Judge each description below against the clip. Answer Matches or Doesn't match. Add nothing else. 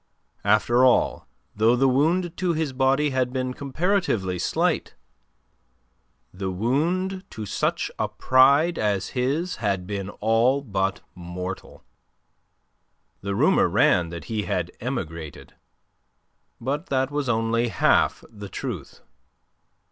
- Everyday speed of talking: Doesn't match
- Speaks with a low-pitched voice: Matches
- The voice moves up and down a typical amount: Doesn't match